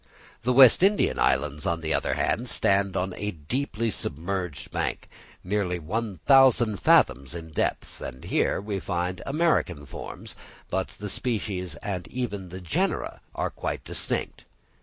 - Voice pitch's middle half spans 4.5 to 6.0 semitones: Yes, average, 5.2 semitones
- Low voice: Yes, very low, 95 Hz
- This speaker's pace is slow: No, average, 145 wpm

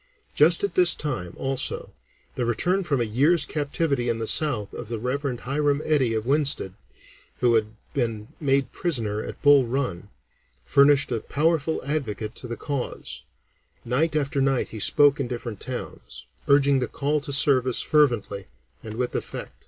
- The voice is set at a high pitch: No, low, 135 Hz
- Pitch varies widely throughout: No, average, 3.8 semitones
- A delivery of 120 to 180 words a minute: Yes, average, 160 wpm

